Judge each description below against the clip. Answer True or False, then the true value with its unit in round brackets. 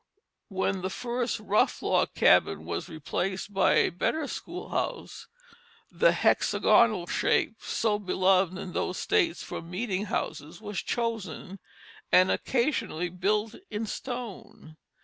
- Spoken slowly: True (120 wpm)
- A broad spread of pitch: False (4.1 semitones)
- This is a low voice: False (200 Hz)